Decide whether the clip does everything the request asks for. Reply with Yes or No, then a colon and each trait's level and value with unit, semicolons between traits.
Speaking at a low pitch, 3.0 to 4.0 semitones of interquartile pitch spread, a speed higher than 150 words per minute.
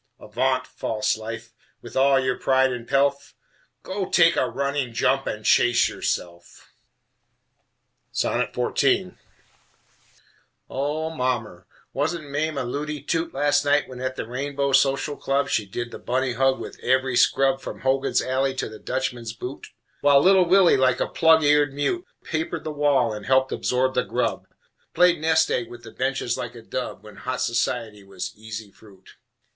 Yes: low, 130 Hz; average, 3.3 semitones; average, 160 wpm